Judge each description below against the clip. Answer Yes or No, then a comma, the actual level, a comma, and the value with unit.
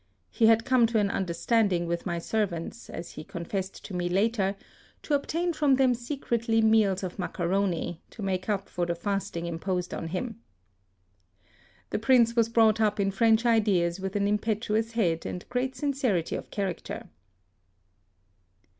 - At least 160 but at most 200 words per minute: Yes, average, 165 wpm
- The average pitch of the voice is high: Yes, high, 205 Hz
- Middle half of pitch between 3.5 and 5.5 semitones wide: Yes, average, 4.2 semitones